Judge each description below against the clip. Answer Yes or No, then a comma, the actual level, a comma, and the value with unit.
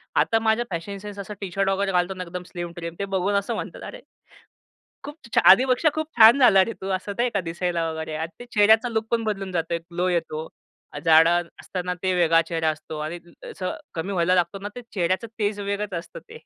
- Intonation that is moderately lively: Yes, average, 3.6 semitones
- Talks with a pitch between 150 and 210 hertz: Yes, high, 190 Hz